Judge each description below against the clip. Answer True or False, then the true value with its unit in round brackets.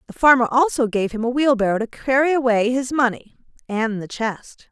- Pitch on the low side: False (240 Hz)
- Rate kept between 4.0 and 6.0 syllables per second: True (5.3 syllables/s)